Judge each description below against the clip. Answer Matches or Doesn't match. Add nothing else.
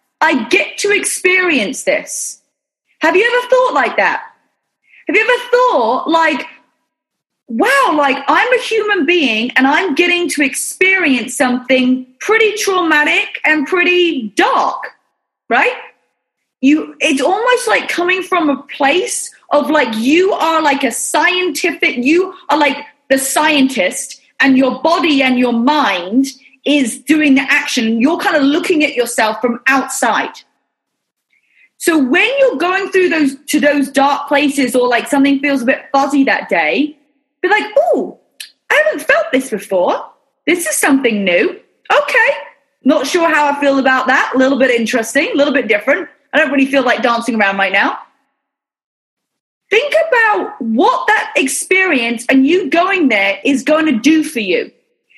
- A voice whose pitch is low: Doesn't match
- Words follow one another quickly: Doesn't match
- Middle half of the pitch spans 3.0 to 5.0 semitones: Matches